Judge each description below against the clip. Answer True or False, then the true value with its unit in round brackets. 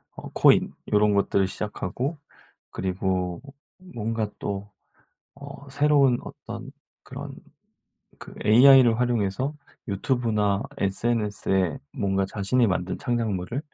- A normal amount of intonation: True (4.5 semitones)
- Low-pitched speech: True (110 Hz)